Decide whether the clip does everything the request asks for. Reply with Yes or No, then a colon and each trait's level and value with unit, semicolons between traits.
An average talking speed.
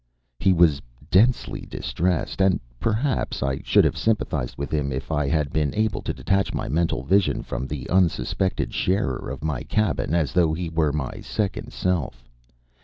Yes: average, 170 wpm